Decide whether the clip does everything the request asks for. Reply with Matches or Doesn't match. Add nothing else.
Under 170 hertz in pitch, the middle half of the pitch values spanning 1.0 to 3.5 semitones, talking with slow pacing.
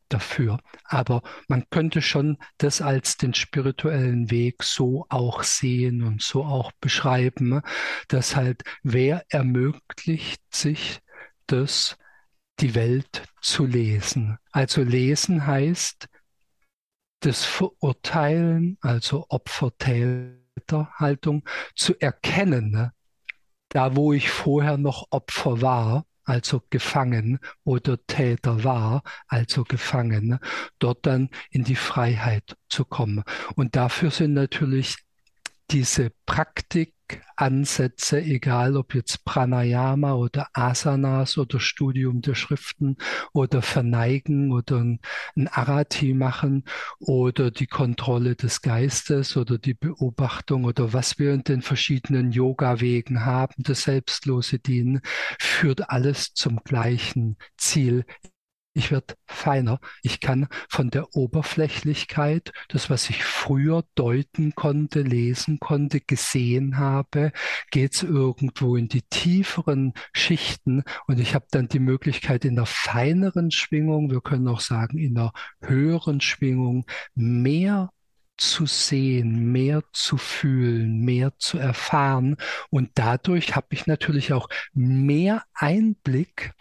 Matches